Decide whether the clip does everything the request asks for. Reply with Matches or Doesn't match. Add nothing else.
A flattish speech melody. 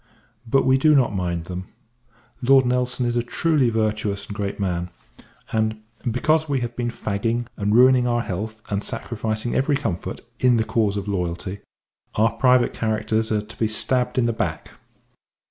Doesn't match